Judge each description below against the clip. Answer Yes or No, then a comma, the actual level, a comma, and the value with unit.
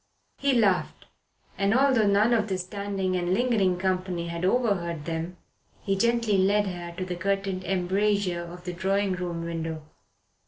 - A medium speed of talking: Yes, average, 155 wpm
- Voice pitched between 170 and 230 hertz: Yes, high, 190 Hz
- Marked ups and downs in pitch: No, narrow, 2.4 semitones